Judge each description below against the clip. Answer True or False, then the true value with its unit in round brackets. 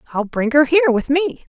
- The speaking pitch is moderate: False (280 Hz)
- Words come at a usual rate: False (230 wpm)